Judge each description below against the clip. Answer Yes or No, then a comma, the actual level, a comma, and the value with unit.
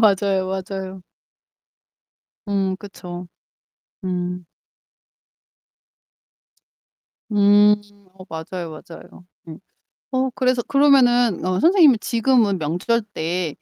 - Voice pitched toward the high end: Yes, high, 195 Hz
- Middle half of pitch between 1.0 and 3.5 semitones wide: No, average, 4.6 semitones